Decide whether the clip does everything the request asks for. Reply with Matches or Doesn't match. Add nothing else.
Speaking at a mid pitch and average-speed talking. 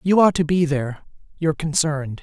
Matches